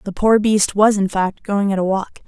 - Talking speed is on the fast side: Yes, fast, 265 wpm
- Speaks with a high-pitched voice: Yes, high, 200 Hz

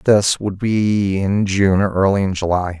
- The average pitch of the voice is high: No, low, 100 Hz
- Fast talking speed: No, average, 195 wpm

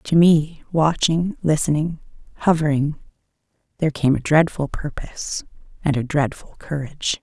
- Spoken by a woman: Yes, female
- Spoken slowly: Yes, slow, 115 wpm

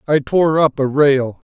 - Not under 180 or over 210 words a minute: Yes, average, 200 wpm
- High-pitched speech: No, medium, 140 Hz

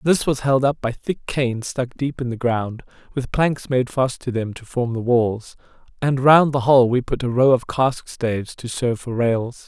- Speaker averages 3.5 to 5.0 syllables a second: Yes, 4.7 syllables/s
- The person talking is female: No, male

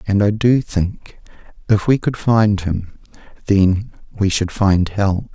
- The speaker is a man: Yes, male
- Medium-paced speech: Yes, average, 155 wpm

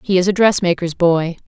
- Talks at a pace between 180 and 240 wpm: Yes, fast, 205 wpm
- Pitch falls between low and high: Yes, medium, 180 Hz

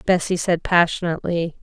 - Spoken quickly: No, slow, 110 wpm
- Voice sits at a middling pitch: Yes, medium, 170 Hz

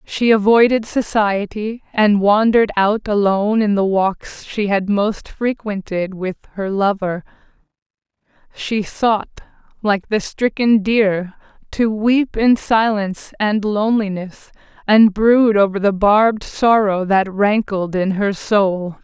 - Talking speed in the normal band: No, slow, 125 wpm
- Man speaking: No, female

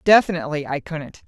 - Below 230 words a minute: Yes, average, 140 wpm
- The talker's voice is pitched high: No, medium, 160 Hz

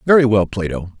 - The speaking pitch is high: No, low, 110 Hz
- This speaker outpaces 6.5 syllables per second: No, 5.9 syllables/s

